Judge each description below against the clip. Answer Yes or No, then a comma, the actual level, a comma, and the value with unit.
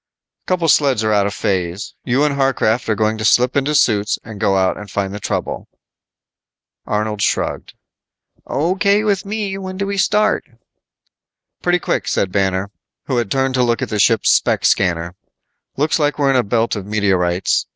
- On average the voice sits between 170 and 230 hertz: No, low, 115 Hz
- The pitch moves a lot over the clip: Yes, wide, 6.6 semitones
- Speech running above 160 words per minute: Yes, average, 180 wpm